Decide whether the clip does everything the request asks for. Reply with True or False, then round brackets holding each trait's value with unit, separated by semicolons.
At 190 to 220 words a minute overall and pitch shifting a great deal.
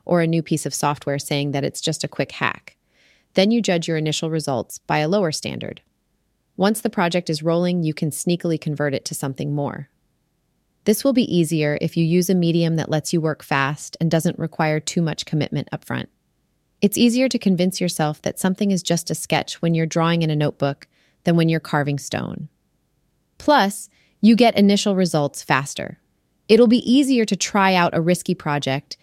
False (195 wpm; 3.7 semitones)